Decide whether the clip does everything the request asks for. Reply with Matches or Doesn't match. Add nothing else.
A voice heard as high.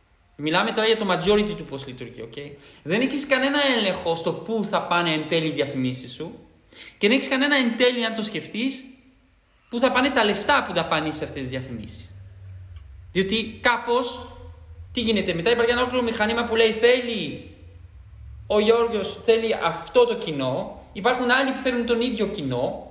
Matches